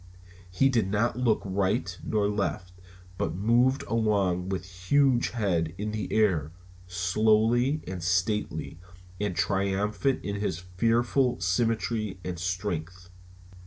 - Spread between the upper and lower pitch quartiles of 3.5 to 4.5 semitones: Yes, average, 3.9 semitones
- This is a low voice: Yes, low, 100 Hz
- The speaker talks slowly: Yes, slow, 120 wpm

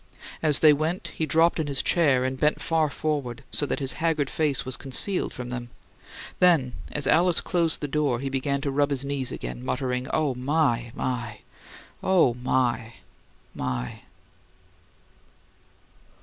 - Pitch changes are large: No, average, 3.7 semitones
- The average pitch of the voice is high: No, medium, 140 Hz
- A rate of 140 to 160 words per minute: Yes, average, 150 wpm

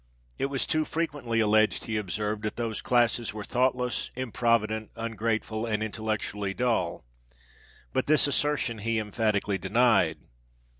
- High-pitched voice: No, low, 110 Hz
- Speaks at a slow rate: Yes, slow, 130 wpm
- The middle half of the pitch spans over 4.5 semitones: No, narrow, 2.4 semitones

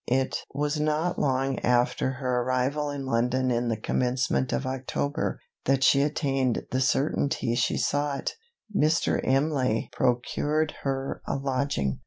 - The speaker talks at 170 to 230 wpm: No, slow, 135 wpm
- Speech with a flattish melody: Yes, narrow, 2.2 semitones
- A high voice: No, low, 135 Hz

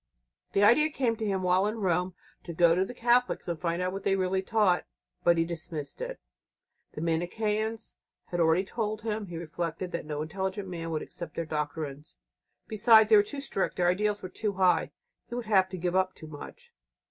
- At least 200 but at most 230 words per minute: Yes, fast, 205 wpm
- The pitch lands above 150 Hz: Yes, medium, 185 Hz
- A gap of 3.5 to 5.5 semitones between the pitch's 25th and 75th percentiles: Yes, average, 4.0 semitones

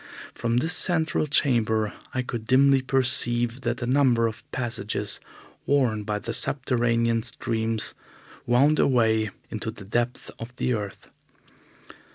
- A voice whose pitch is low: Yes, low, 120 Hz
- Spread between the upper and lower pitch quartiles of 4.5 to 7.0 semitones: No, average, 2.7 semitones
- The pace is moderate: No, slow, 130 wpm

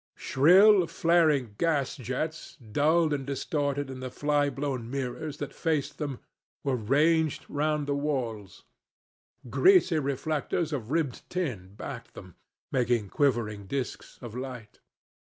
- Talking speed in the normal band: No, slow, 125 wpm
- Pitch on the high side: No, medium, 140 Hz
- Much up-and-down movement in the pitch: No, average, 3.8 semitones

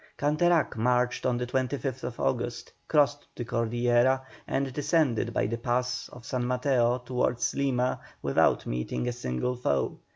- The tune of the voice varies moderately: No, narrow, 1.7 semitones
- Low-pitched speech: Yes, low, 125 Hz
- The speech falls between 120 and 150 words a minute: Yes, average, 140 wpm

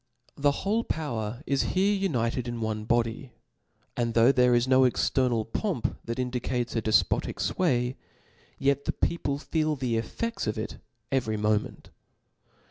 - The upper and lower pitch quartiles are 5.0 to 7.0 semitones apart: No, average, 3.6 semitones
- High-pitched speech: No, low, 125 Hz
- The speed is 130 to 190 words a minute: Yes, average, 150 wpm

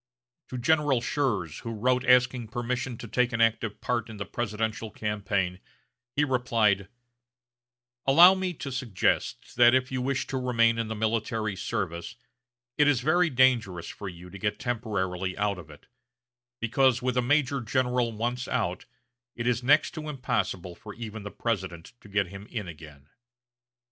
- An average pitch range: Yes, average, 3.8 semitones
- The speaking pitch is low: Yes, low, 115 Hz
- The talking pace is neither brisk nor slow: Yes, average, 165 wpm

